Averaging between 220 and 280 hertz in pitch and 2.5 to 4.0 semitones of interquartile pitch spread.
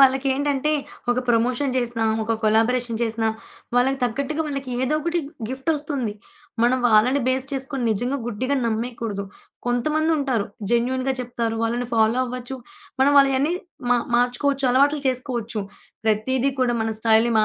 Yes: very high, 250 Hz; average, 2.8 semitones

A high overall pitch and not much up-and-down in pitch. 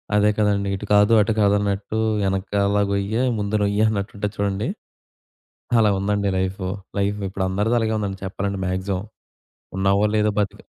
No: low, 100 Hz; narrow, 1.1 semitones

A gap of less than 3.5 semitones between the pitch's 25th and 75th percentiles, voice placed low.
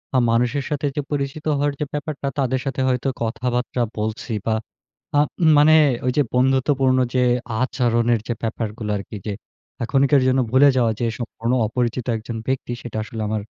Yes: average, 2.9 semitones; low, 125 Hz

